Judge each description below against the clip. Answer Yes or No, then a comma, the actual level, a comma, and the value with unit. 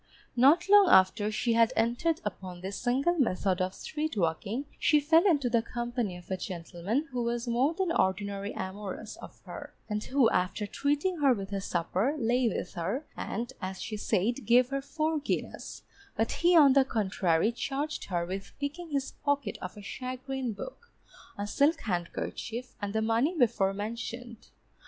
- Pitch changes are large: Yes, wide, 6.1 semitones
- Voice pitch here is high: Yes, high, 235 Hz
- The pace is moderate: Yes, average, 170 wpm